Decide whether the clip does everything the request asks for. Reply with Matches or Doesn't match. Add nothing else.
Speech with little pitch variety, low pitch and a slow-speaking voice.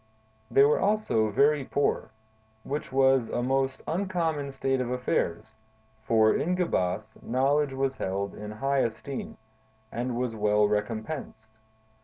Doesn't match